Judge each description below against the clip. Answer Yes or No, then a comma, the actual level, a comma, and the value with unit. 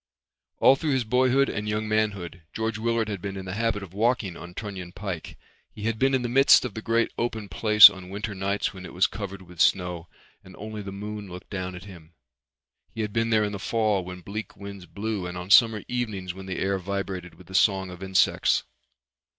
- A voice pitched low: Yes, low, 100 Hz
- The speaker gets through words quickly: Yes, fast, 220 wpm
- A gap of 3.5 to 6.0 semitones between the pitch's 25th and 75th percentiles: No, average, 3.0 semitones